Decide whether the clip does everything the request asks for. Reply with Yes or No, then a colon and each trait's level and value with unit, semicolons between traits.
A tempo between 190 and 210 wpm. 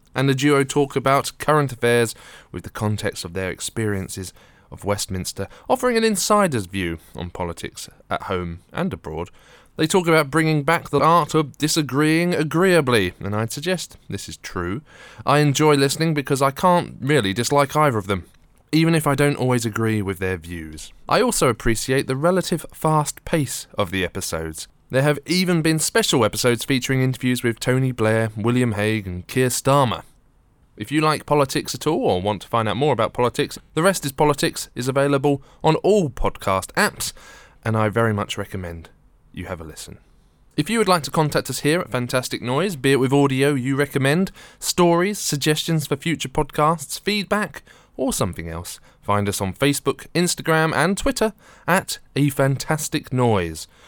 No: average, 175 wpm